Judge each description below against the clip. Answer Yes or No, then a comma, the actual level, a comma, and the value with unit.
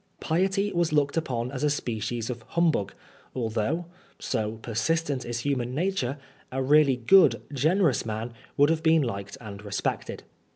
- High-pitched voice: No, low, 135 Hz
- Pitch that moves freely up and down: Yes, wide, 5.7 semitones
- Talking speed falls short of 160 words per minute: Yes, average, 150 wpm